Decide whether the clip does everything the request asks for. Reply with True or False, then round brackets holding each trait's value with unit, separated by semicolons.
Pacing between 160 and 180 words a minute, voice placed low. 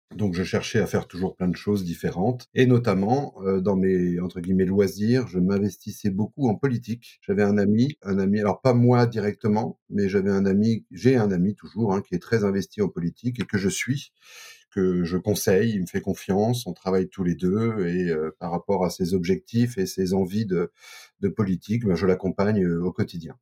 False (210 wpm; 100 Hz)